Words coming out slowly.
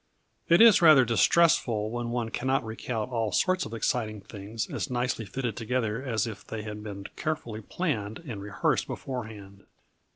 No: average, 165 wpm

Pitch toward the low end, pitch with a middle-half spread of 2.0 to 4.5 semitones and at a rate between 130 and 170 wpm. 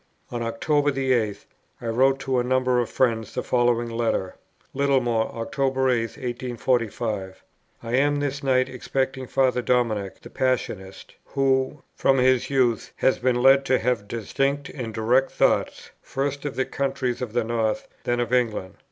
Yes: low, 125 Hz; narrow, 2.4 semitones; average, 160 wpm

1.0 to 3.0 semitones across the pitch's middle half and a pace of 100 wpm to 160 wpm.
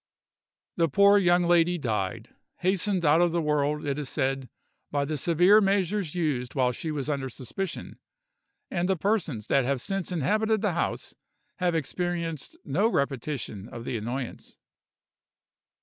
No: average, 5.0 semitones; average, 150 wpm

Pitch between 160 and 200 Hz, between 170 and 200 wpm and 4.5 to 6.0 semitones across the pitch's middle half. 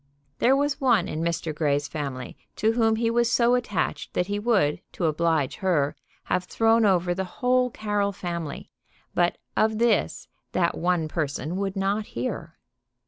No: high, 190 Hz; average, 160 wpm; wide, 5.4 semitones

